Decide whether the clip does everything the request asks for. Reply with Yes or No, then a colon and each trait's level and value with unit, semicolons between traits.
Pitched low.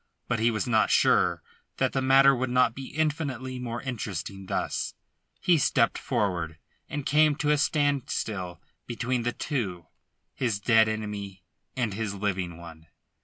Yes: low, 115 Hz